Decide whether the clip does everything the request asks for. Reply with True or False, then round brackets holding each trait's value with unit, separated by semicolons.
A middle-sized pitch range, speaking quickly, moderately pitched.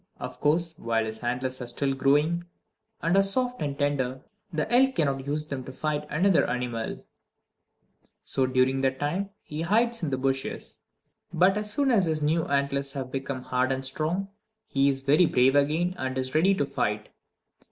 False (4.3 semitones; 180 wpm; 145 Hz)